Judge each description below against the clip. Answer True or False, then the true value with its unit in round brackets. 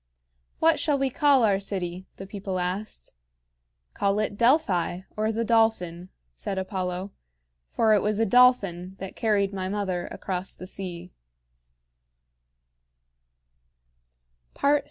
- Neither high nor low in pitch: False (195 Hz)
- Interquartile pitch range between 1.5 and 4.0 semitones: True (3.3 semitones)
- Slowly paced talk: True (115 wpm)